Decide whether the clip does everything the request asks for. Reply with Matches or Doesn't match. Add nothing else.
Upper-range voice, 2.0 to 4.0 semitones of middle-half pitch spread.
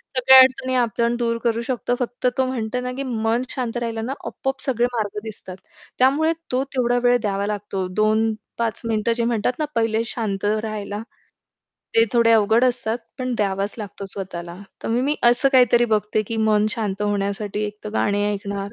Matches